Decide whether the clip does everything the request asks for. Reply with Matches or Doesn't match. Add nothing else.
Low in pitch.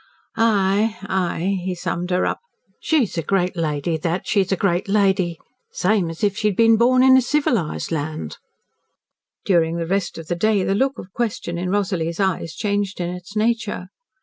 Doesn't match